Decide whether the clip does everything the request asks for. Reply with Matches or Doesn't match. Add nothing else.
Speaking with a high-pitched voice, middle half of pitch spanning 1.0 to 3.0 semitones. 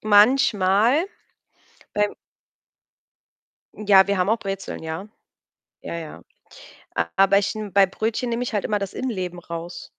Matches